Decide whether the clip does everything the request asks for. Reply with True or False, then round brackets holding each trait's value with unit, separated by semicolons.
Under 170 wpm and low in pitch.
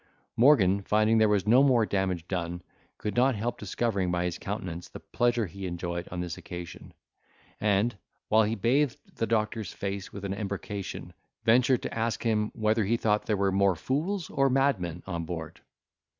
False (175 wpm; 105 Hz)